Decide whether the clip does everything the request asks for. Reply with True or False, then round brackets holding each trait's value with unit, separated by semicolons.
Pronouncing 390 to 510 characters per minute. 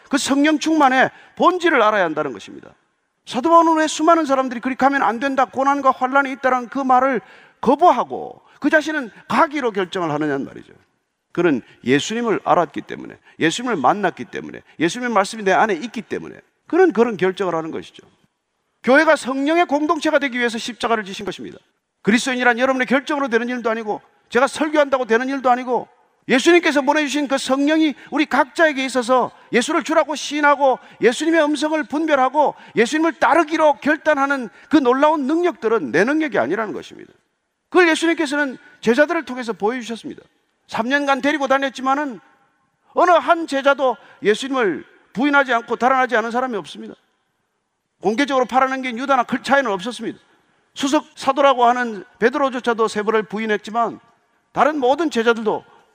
True (395 characters per minute)